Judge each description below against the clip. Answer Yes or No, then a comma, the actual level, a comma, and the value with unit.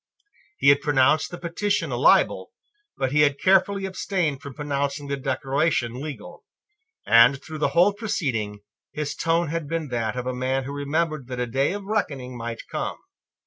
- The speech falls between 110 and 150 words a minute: No, average, 175 wpm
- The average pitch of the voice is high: No, medium, 140 Hz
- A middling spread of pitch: Yes, average, 4.4 semitones